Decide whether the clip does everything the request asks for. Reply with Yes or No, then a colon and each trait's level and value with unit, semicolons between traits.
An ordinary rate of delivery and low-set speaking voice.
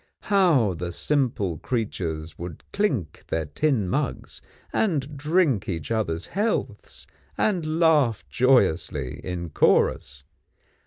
No: slow, 105 wpm; low, 115 Hz